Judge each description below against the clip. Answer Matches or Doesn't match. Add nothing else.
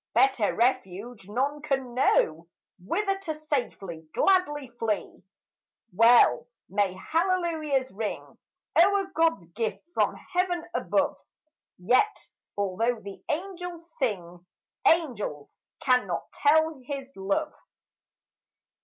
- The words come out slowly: Matches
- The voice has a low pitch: Doesn't match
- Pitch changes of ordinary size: Doesn't match